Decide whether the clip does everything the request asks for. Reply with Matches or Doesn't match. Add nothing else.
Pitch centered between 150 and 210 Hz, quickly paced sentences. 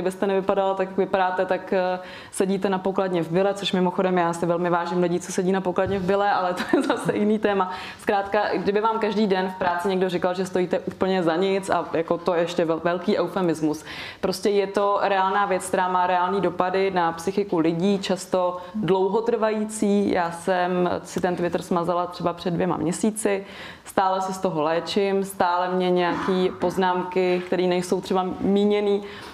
Matches